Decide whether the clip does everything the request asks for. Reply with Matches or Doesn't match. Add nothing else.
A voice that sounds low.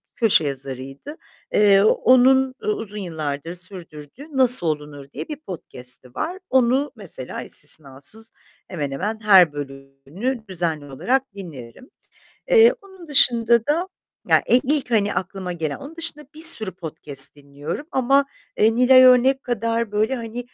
Doesn't match